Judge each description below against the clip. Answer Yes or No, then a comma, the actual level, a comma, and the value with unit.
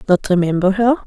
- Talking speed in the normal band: Yes, average, 170 wpm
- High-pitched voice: Yes, high, 200 Hz